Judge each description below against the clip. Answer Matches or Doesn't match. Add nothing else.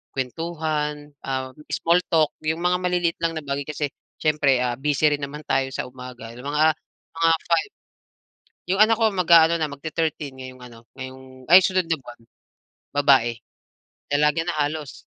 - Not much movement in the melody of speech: Doesn't match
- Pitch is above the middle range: Doesn't match